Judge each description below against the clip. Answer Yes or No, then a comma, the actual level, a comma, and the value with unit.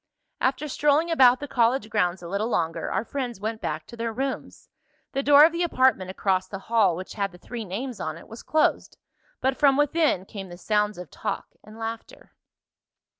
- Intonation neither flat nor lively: No, wide, 5.8 semitones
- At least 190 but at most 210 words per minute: Yes, average, 195 wpm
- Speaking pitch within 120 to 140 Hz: No, high, 225 Hz